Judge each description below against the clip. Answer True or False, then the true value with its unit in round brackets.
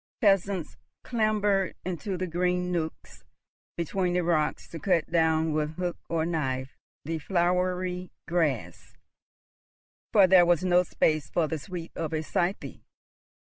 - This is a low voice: False (175 Hz)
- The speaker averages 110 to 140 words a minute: True (135 wpm)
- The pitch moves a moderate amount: False (2.3 semitones)